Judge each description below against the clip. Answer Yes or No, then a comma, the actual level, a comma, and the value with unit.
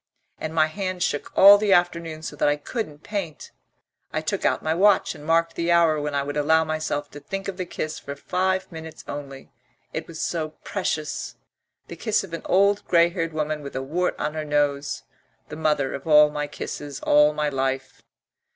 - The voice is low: No, medium, 155 Hz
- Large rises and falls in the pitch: No, average, 3.1 semitones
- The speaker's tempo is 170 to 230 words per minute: Yes, average, 200 wpm